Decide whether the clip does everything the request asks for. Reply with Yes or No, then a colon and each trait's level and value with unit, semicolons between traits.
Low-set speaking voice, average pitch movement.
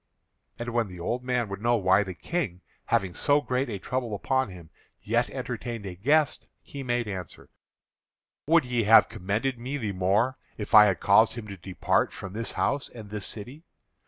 Yes: low, 115 Hz; average, 4.3 semitones